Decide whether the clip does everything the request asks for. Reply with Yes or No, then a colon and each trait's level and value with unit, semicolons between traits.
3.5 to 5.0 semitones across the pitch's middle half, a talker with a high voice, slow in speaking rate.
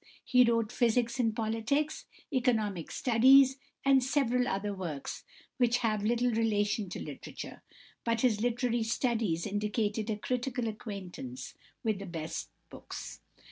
No: average, 3.1 semitones; high, 225 Hz; slow, 130 wpm